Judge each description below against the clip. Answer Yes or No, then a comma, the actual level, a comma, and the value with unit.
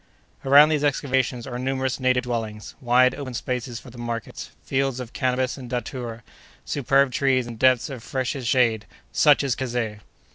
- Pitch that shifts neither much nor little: No, narrow, 1.9 semitones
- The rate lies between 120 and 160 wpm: Yes, average, 155 wpm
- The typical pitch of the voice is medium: No, low, 125 Hz